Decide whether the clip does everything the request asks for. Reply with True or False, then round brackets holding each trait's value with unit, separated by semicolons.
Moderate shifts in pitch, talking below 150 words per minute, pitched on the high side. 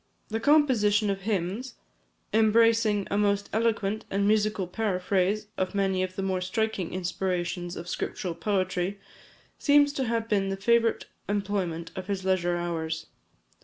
True (3.0 semitones; 140 wpm; 200 Hz)